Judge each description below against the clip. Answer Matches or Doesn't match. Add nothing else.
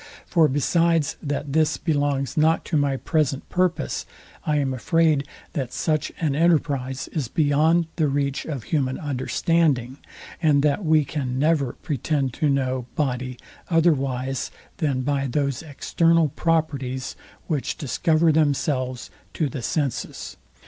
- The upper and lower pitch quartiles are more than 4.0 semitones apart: Doesn't match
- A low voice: Doesn't match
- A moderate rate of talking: Doesn't match